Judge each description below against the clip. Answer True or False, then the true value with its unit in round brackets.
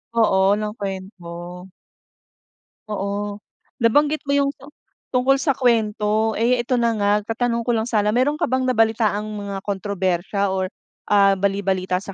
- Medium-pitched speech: False (210 Hz)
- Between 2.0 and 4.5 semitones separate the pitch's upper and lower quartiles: True (3.3 semitones)